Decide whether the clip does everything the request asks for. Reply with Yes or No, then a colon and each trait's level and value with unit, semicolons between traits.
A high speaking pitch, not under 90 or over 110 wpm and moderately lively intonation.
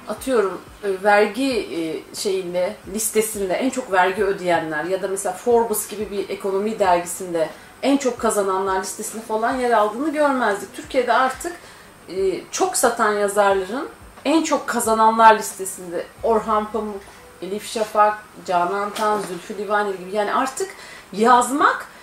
No: high, 215 Hz; average, 125 wpm; average, 3.9 semitones